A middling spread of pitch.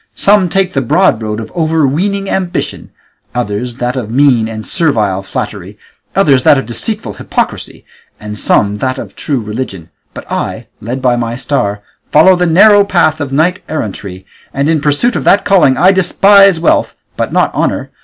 No: wide, 8.2 semitones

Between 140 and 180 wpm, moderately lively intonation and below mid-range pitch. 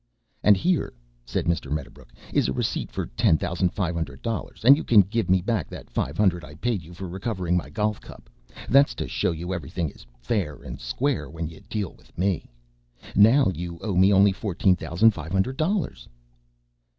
No: average, 200 wpm; average, 4.6 semitones; very low, 90 Hz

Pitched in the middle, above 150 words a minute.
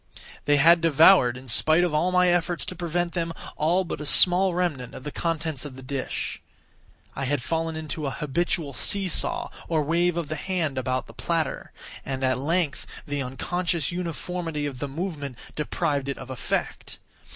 Yes: medium, 155 Hz; average, 180 wpm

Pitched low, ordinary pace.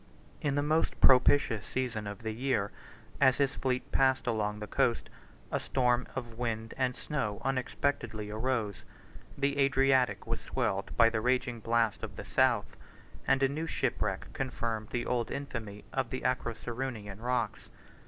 Yes: low, 125 Hz; average, 155 wpm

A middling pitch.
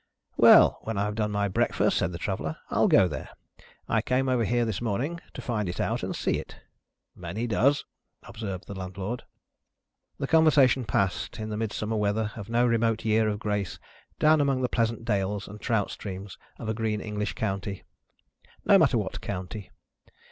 No: low, 110 Hz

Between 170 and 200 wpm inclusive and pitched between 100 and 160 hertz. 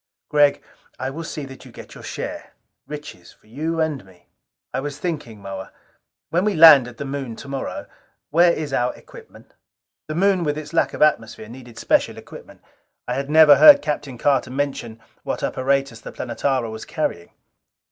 Yes: average, 175 wpm; medium, 140 Hz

